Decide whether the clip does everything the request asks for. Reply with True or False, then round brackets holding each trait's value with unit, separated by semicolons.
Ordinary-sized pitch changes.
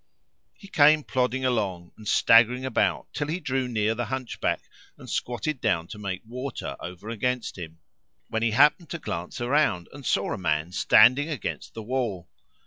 True (4.8 semitones)